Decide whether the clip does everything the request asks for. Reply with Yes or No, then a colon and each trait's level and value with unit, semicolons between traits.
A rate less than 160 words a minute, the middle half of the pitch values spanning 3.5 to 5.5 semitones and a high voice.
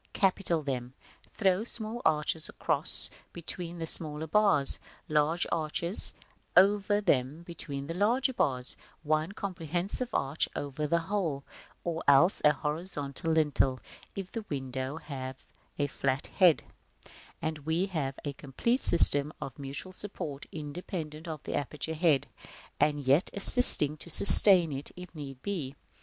No: slow, 135 wpm; average, 4.2 semitones; medium, 155 Hz